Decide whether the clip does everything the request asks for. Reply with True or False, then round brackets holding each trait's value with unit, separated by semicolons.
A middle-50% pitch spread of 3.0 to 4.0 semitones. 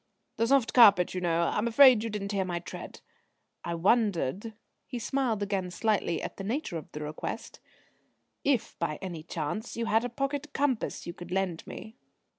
False (5.3 semitones)